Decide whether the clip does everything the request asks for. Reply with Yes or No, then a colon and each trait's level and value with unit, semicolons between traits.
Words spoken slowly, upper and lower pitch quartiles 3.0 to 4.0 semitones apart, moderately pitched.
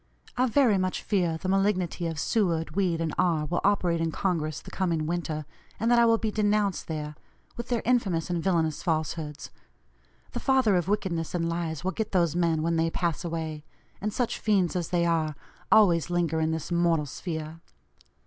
No: average, 185 wpm; average, 3.4 semitones; medium, 170 Hz